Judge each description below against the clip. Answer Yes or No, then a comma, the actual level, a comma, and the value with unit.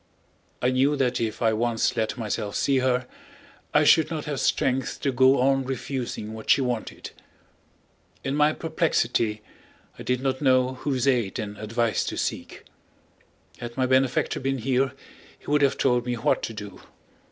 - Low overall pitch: Yes, low, 130 Hz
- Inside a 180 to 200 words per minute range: No, average, 165 wpm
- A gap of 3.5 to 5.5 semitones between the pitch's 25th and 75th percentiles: No, narrow, 2.5 semitones